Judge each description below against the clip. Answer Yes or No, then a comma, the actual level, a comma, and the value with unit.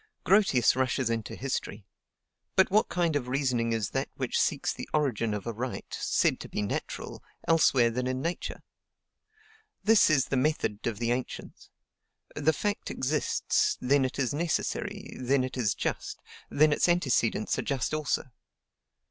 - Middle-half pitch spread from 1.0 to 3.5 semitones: No, average, 4.4 semitones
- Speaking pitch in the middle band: No, low, 130 Hz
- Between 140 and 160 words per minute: Yes, average, 155 wpm